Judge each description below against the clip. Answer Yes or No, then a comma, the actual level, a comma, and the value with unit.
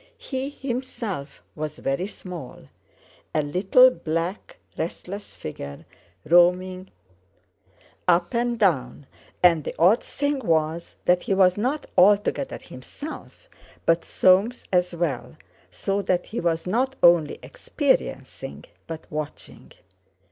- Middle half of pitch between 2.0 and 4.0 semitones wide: No, average, 4.7 semitones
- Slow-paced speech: Yes, slow, 110 wpm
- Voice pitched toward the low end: No, medium, 180 Hz